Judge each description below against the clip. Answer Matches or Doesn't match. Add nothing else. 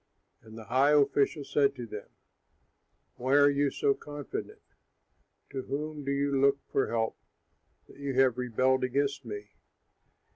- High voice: Doesn't match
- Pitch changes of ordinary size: Doesn't match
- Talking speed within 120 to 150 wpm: Matches